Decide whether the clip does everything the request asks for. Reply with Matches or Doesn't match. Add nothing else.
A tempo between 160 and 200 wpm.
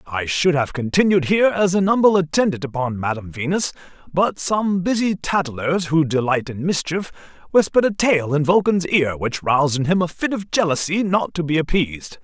Matches